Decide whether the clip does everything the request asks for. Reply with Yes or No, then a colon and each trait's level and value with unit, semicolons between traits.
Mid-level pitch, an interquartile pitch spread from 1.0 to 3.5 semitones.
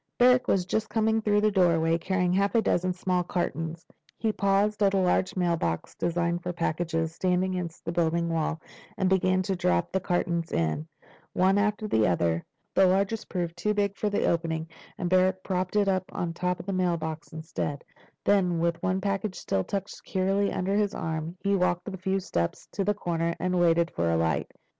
Yes: medium, 180 Hz; average, 2.7 semitones